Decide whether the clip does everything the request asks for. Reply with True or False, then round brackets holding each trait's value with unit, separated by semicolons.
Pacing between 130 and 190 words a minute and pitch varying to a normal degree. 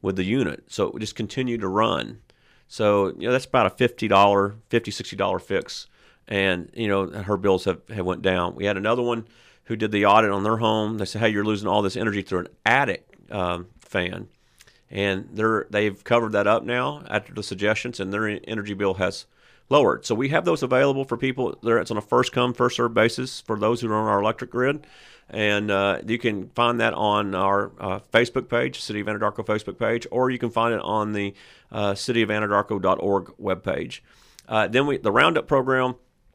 False (205 wpm; 3.1 semitones)